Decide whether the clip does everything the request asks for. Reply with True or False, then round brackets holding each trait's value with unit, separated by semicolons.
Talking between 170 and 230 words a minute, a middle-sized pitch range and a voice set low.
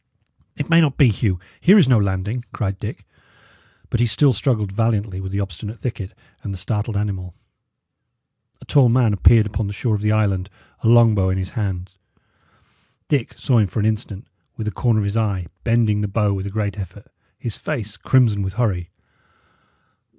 True (190 wpm; 3.0 semitones; 105 Hz)